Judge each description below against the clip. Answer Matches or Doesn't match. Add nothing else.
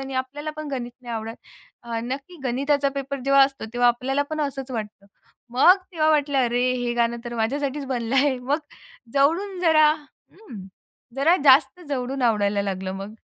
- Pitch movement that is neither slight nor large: Matches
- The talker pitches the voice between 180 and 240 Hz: Doesn't match